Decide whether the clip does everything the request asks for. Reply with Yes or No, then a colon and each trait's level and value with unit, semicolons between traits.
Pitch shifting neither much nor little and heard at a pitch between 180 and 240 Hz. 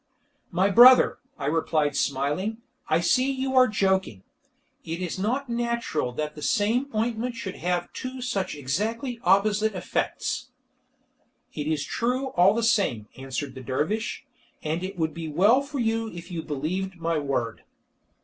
No: wide, 7.0 semitones; high, 190 Hz